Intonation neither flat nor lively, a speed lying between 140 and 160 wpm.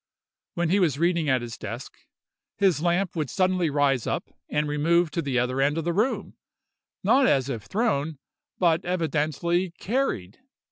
Yes: average, 4.3 semitones; average, 155 wpm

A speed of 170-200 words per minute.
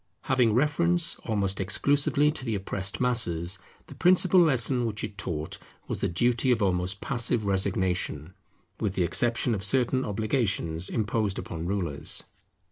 No: average, 140 wpm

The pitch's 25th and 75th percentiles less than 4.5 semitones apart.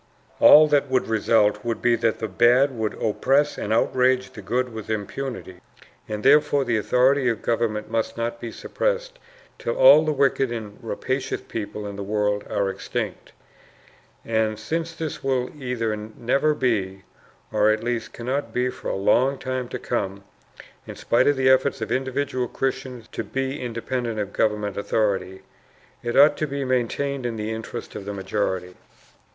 Yes: average, 3.8 semitones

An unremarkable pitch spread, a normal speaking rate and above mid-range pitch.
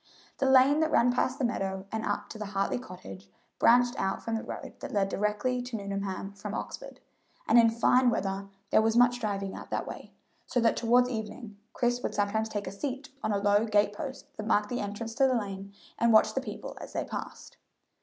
No: average, 3.5 semitones; fast, 215 wpm; high, 220 Hz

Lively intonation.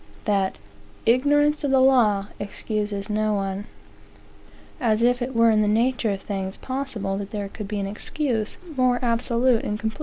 No: average, 3.6 semitones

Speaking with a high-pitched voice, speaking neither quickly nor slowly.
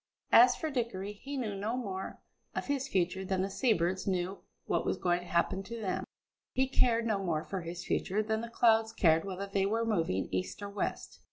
No: high, 200 Hz; fast, 210 wpm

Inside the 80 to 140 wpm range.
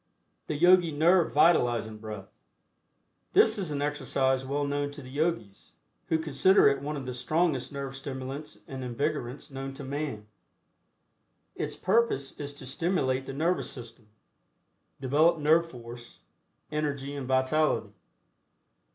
Yes: slow, 135 wpm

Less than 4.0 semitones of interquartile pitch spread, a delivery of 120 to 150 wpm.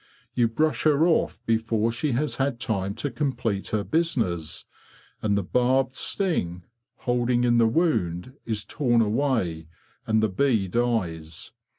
No: average, 4.6 semitones; average, 145 wpm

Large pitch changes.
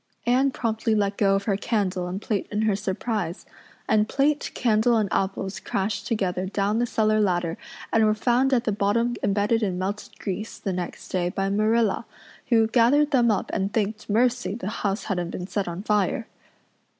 No: average, 2.8 semitones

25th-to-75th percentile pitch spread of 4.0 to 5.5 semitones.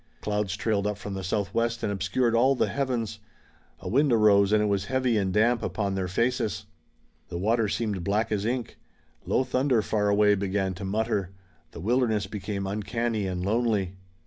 No: average, 2.8 semitones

